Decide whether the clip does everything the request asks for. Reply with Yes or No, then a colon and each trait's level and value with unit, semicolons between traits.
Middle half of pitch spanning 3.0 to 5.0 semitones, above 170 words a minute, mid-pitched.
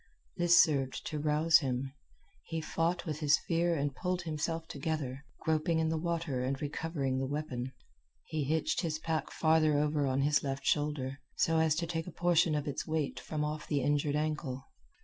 No: narrow, 2.4 semitones; average, 185 wpm; medium, 155 Hz